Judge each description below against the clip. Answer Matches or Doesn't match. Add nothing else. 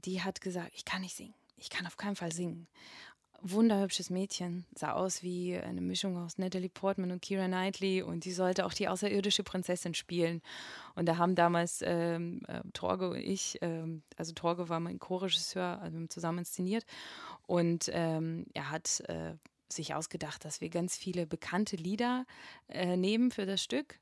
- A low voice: Doesn't match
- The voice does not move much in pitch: Matches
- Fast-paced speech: Doesn't match